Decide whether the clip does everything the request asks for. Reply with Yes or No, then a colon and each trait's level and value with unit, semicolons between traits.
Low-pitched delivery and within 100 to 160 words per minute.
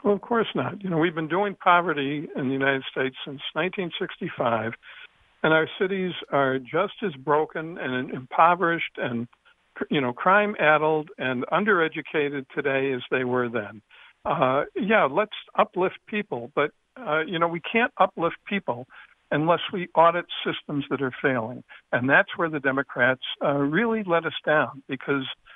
No: medium, 155 Hz; average, 155 wpm